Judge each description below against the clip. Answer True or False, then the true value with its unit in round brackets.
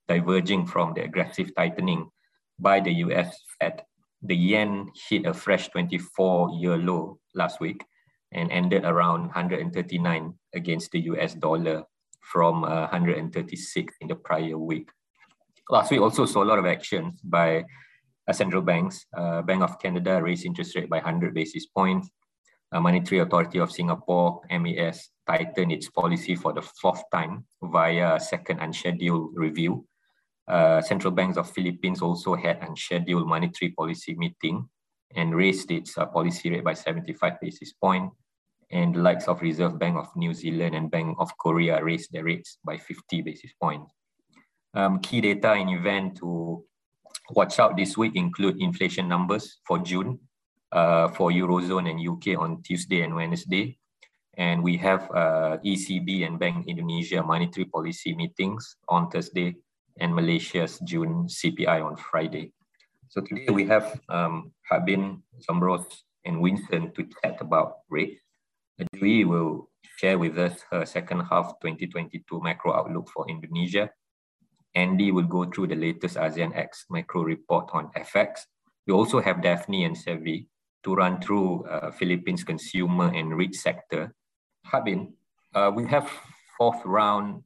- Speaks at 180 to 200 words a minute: False (145 wpm)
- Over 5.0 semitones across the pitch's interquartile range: False (3.6 semitones)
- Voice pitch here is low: True (90 Hz)